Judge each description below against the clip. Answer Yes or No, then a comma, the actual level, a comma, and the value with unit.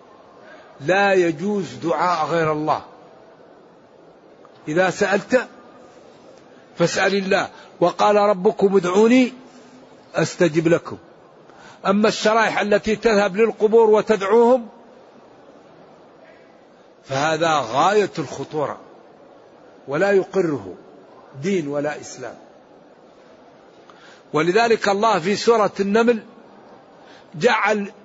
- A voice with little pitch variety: No, average, 3.8 semitones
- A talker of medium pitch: No, high, 200 Hz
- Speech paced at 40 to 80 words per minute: Yes, average, 75 wpm